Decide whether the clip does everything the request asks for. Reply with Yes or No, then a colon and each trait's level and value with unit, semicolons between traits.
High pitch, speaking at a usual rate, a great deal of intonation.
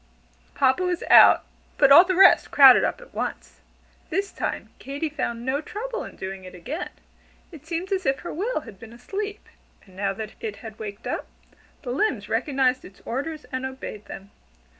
Yes: very high, 265 Hz; average, 180 wpm; wide, 7.8 semitones